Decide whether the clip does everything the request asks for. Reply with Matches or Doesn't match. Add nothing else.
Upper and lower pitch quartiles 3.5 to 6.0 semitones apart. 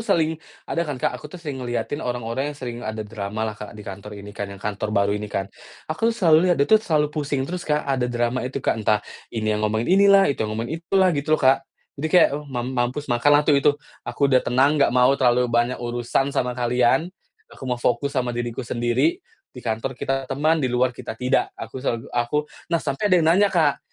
Matches